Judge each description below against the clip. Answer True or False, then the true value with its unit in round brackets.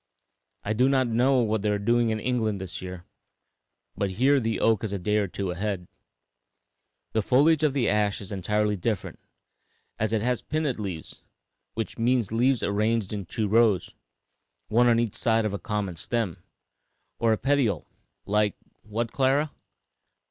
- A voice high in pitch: False (110 Hz)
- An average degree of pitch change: True (3.0 semitones)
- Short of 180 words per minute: True (165 wpm)